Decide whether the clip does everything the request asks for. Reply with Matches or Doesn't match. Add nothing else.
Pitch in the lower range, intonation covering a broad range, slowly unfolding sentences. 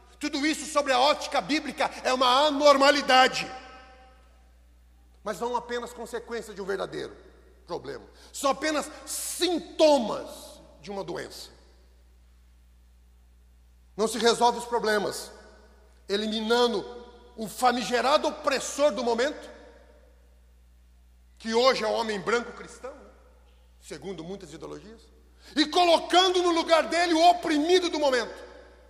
Doesn't match